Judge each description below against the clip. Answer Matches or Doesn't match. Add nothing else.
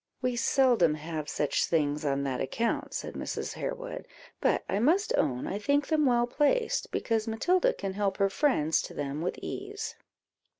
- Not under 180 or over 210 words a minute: Doesn't match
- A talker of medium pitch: Doesn't match